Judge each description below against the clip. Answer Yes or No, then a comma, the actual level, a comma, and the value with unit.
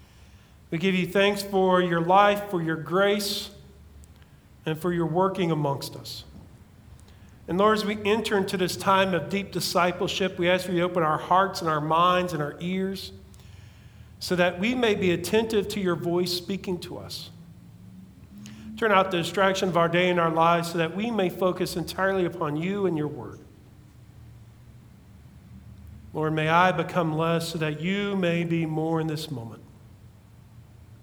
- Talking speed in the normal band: Yes, average, 170 wpm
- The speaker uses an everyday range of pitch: No, wide, 8.5 semitones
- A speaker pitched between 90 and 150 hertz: No, medium, 170 Hz